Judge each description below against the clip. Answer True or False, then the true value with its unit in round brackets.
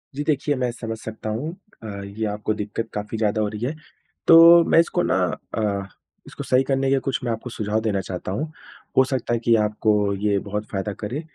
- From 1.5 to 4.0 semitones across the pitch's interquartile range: True (3.7 semitones)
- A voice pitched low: True (110 Hz)